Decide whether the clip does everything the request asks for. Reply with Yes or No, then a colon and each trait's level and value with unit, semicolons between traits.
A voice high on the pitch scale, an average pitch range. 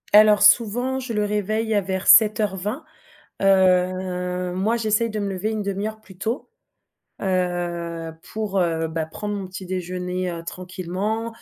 Yes: high, 195 Hz; average, 3.0 semitones